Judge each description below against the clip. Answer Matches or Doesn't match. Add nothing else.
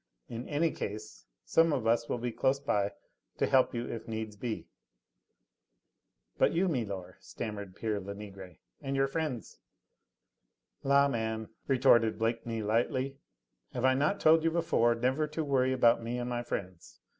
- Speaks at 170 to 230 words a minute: Doesn't match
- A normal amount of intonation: Matches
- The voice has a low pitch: Matches